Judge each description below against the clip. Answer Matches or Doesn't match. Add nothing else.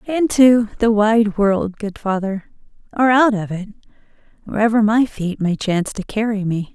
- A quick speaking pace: Doesn't match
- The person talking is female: Matches